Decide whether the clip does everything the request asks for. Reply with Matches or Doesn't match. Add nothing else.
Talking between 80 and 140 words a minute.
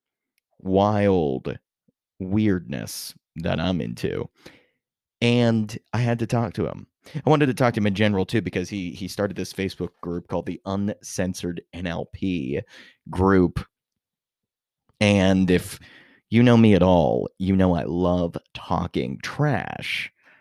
Matches